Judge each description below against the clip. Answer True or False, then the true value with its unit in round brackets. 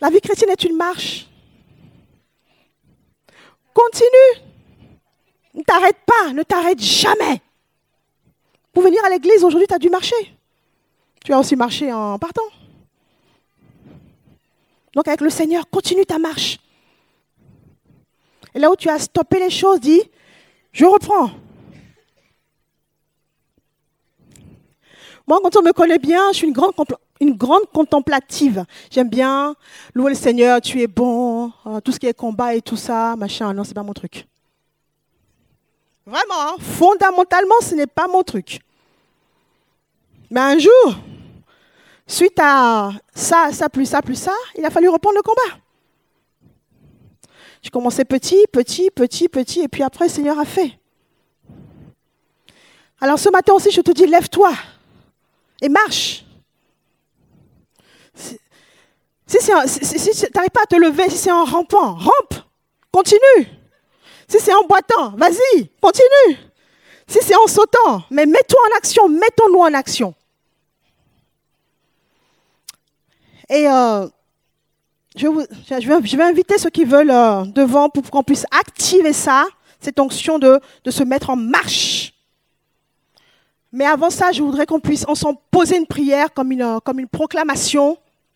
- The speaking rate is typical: False (140 wpm)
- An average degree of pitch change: False (5.9 semitones)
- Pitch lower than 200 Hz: False (320 Hz)